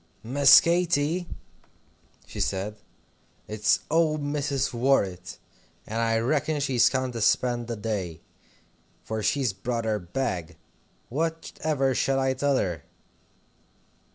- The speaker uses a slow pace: Yes, slow, 120 wpm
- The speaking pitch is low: Yes, low, 125 Hz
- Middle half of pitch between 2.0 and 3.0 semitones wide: No, average, 5.0 semitones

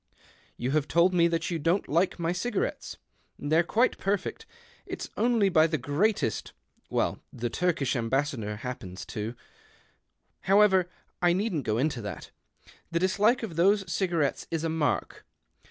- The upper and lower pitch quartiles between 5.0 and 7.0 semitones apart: Yes, wide, 5.5 semitones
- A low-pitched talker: No, medium, 170 Hz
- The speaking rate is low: No, average, 150 wpm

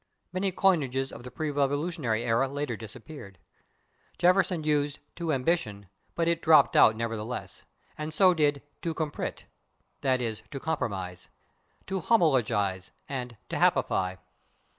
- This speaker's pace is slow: Yes, slow, 130 wpm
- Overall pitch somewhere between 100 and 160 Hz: Yes, medium, 140 Hz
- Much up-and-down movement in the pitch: Yes, wide, 5.9 semitones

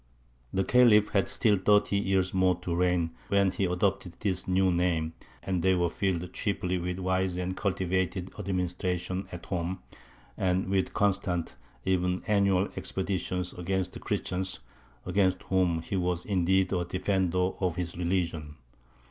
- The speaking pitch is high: No, very low, 90 Hz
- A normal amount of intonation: No, narrow, 1.2 semitones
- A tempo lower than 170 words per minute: Yes, average, 150 wpm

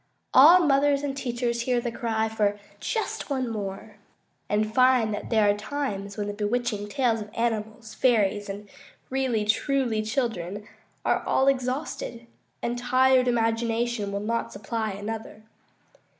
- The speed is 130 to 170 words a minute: Yes, average, 140 wpm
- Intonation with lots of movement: No, average, 3.4 semitones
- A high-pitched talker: Yes, high, 230 Hz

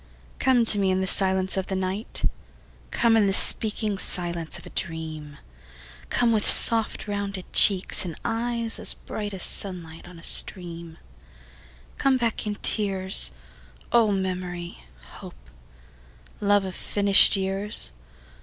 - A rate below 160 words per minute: Yes, slow, 135 wpm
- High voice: Yes, high, 195 Hz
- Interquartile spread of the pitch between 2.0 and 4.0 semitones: Yes, average, 2.9 semitones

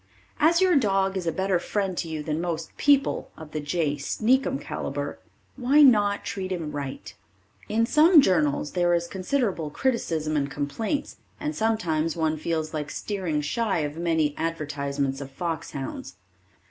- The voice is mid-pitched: Yes, medium, 170 Hz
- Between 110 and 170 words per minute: Yes, average, 160 wpm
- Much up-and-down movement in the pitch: Yes, wide, 6.3 semitones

